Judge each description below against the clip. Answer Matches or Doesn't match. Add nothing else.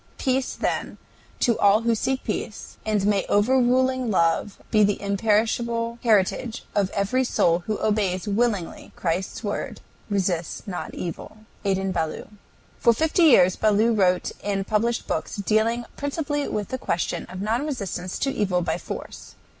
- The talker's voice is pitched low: Doesn't match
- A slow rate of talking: Doesn't match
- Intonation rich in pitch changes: Doesn't match